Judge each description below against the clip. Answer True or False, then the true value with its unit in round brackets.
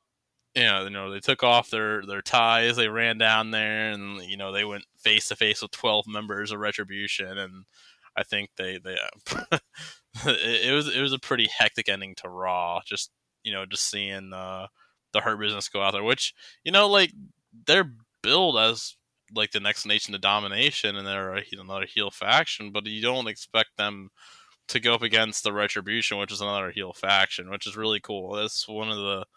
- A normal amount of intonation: False (2.3 semitones)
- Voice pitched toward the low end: True (105 Hz)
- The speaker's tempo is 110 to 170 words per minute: False (200 wpm)